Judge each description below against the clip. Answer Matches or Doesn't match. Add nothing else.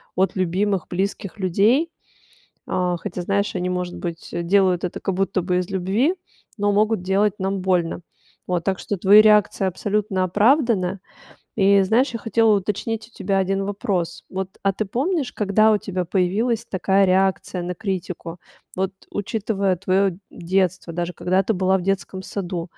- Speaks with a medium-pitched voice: Doesn't match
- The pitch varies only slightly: Matches